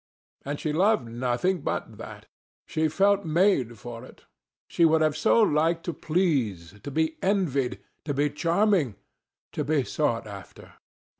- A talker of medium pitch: Yes, medium, 155 Hz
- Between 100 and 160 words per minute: Yes, average, 150 wpm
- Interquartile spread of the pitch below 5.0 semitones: No, wide, 5.5 semitones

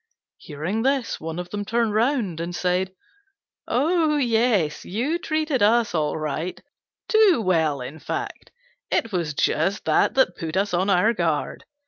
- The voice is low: No, high, 200 Hz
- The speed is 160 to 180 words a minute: No, average, 150 wpm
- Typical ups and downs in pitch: No, wide, 6.8 semitones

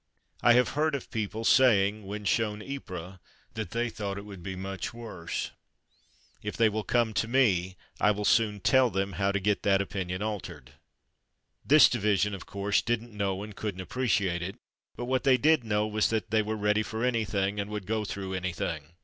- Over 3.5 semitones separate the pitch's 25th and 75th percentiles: No, average, 2.8 semitones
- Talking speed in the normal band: Yes, average, 195 wpm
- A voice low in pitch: Yes, low, 105 Hz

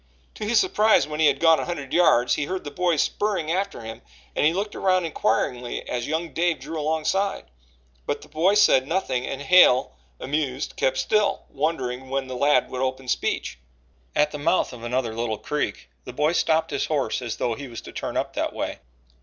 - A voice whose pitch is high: No, medium, 150 Hz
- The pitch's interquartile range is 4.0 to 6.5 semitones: Yes, average, 5.0 semitones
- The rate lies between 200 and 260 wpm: Yes, fast, 205 wpm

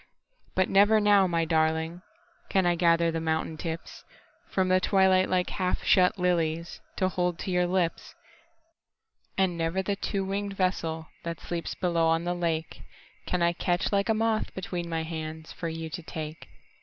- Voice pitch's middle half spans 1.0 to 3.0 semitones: Yes, narrow, 2.5 semitones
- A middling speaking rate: Yes, average, 145 wpm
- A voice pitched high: No, medium, 175 Hz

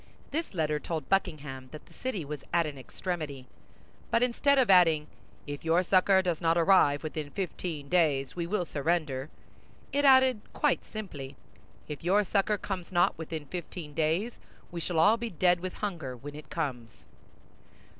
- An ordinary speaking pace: Yes, average, 165 wpm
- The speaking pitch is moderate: Yes, medium, 170 Hz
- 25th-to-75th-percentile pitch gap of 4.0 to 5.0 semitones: Yes, average, 4.4 semitones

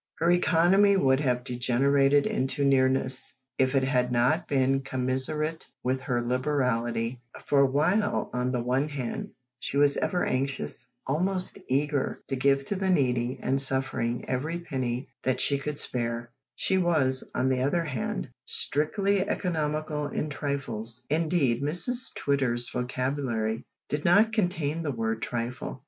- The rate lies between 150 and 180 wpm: No, average, 140 wpm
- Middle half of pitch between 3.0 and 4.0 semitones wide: Yes, average, 3.4 semitones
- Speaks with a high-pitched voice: No, low, 135 Hz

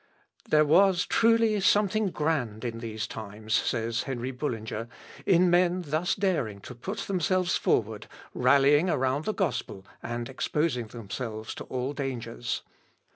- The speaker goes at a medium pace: No, slow, 130 wpm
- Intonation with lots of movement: Yes, wide, 7.6 semitones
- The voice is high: No, low, 135 Hz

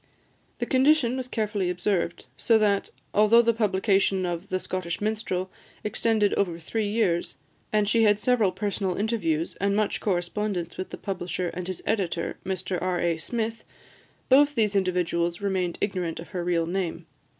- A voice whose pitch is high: Yes, high, 195 Hz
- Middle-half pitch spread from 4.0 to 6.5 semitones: No, average, 3.4 semitones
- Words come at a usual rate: Yes, average, 160 wpm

